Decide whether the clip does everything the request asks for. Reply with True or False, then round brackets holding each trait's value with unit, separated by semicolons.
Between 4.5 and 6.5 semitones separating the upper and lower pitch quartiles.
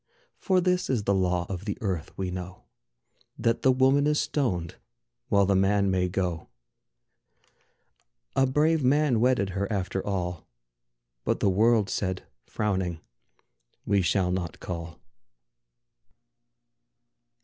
True (5.5 semitones)